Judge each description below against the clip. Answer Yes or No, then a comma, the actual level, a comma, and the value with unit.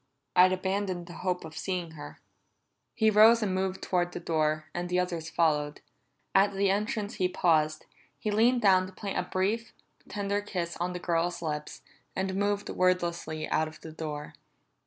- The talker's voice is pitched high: No, medium, 180 Hz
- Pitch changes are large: No, average, 3.2 semitones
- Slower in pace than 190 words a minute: Yes, average, 175 wpm